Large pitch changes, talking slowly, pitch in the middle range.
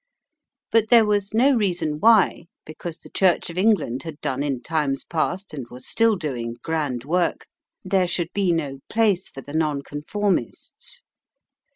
No: wide, 5.7 semitones; average, 155 wpm; medium, 170 Hz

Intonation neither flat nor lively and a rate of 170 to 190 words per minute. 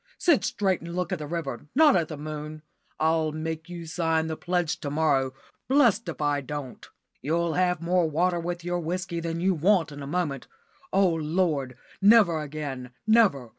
Yes: average, 3.0 semitones; average, 180 wpm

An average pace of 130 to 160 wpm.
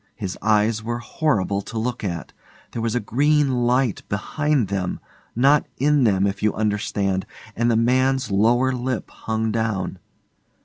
Yes: average, 150 wpm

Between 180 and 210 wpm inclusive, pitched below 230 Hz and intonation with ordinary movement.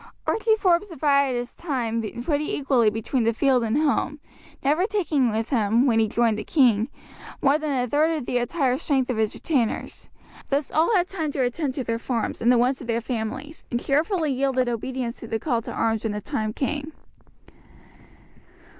No: average, 190 wpm; very high, 260 Hz; average, 4.3 semitones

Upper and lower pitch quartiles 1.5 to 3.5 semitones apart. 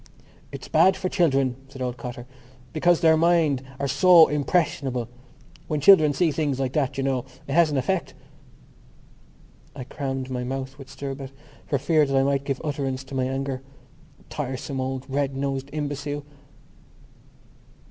Yes: narrow, 2.4 semitones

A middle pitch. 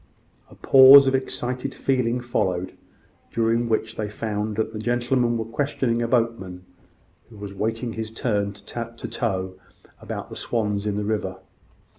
No: low, 115 Hz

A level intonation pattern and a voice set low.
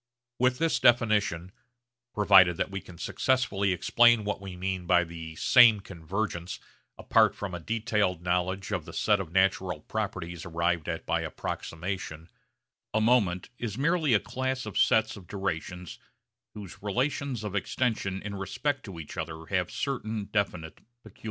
No: average, 3.8 semitones; very low, 95 Hz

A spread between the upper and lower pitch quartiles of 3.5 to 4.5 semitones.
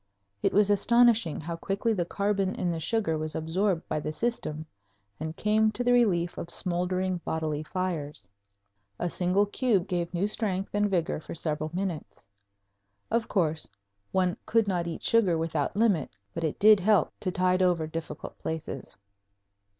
Yes: average, 4.1 semitones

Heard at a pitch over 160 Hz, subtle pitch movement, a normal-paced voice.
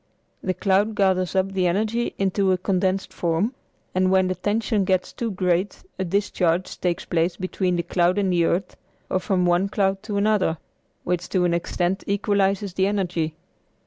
Yes: medium, 185 Hz; narrow, 1.9 semitones; average, 175 wpm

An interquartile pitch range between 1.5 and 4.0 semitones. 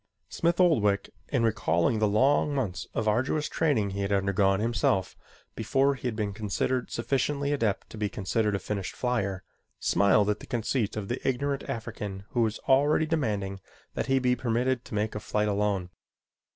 No: average, 4.5 semitones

